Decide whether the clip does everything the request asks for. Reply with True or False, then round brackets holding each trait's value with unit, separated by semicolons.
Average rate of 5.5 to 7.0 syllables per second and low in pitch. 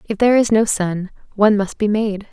False (5.7 syllables/s; 210 Hz)